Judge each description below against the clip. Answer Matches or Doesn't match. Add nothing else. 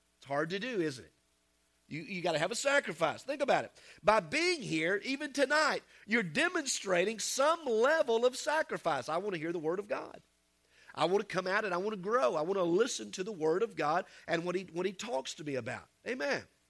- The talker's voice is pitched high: Matches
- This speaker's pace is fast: Matches